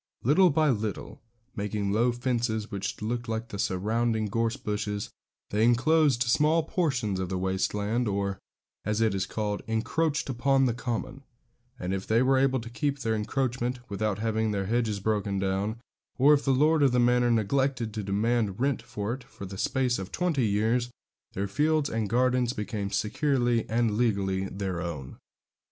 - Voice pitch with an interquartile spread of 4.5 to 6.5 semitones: No, average, 3.8 semitones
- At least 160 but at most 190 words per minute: Yes, average, 175 wpm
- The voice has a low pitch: Yes, low, 115 Hz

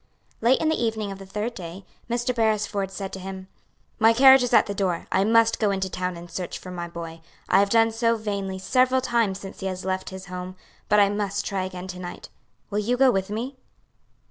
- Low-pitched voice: No, high, 200 Hz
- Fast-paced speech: Yes, fast, 225 wpm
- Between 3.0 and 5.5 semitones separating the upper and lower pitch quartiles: Yes, average, 3.3 semitones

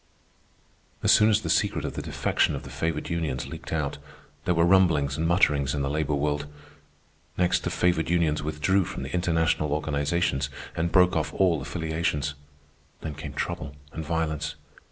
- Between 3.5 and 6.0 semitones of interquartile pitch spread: No, narrow, 2.6 semitones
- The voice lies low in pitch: Yes, very low, 80 Hz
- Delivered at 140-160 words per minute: No, average, 170 wpm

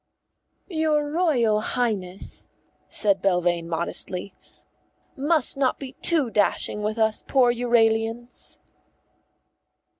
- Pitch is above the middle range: Yes, high, 230 Hz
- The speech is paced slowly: Yes, slow, 90 wpm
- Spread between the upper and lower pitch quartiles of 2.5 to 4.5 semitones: No, average, 5.2 semitones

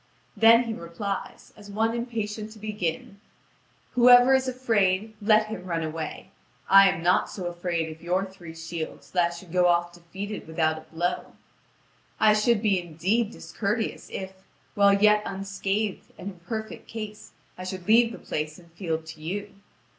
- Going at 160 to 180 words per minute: Yes, average, 165 wpm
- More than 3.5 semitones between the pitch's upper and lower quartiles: Yes, average, 3.9 semitones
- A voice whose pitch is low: No, high, 195 Hz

